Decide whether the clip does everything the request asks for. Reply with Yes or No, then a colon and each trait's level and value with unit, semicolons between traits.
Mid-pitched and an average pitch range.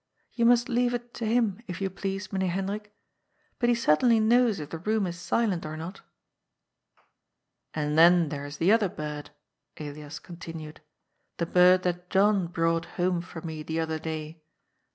Yes: medium, 180 Hz; average, 4.7 semitones